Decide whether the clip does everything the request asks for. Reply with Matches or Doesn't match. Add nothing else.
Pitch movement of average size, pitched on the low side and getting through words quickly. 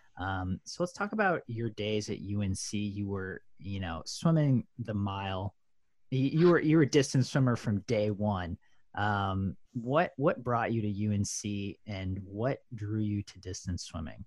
Doesn't match